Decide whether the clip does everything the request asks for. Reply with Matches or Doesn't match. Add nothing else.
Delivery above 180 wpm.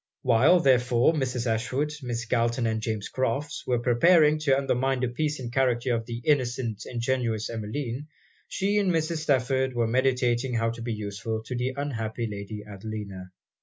Doesn't match